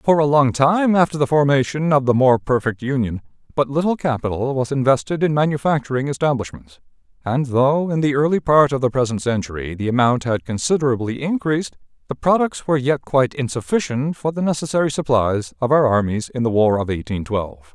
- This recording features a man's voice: Yes, male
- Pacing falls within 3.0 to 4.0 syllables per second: No, 5.8 syllables/s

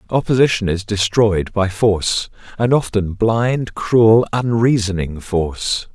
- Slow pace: Yes, slow, 110 wpm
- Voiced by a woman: No, male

